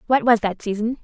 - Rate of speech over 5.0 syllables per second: Yes, 6.0 syllables/s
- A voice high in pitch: Yes, high, 225 Hz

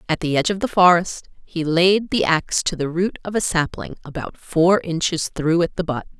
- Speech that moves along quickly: Yes, fast, 225 wpm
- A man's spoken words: No, female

